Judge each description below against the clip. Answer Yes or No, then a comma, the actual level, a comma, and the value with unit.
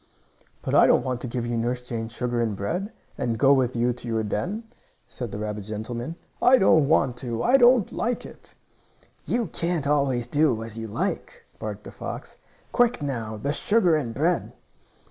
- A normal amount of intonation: No, wide, 6.4 semitones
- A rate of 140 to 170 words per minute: No, average, 185 wpm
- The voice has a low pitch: Yes, low, 125 Hz